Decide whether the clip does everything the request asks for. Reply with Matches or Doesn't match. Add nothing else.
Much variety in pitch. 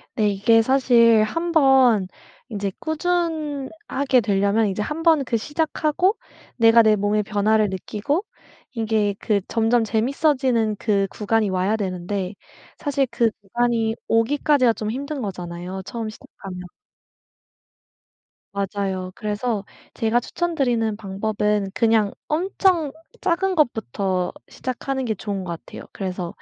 Doesn't match